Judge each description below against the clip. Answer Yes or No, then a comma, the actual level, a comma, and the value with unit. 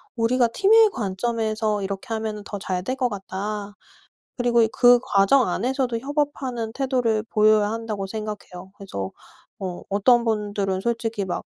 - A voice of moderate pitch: No, high, 220 Hz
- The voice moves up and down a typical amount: Yes, average, 3.4 semitones